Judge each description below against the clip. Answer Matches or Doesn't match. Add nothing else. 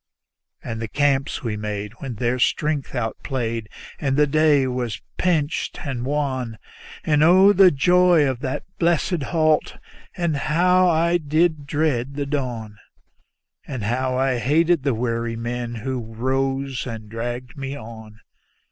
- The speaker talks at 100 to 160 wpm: Matches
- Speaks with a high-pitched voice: Doesn't match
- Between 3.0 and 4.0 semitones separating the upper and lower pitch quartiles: Doesn't match